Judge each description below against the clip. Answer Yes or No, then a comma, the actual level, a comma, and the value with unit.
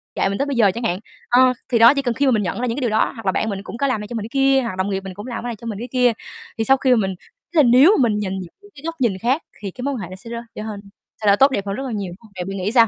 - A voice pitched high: Yes, high, 230 Hz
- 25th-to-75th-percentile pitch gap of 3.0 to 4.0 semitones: No, average, 4.4 semitones